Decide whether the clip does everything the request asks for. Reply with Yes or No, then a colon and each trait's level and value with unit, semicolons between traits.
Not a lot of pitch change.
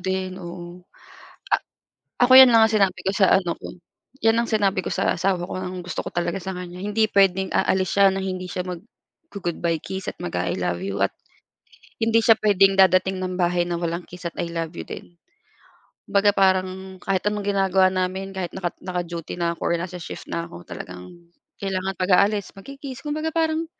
Yes: narrow, 2.3 semitones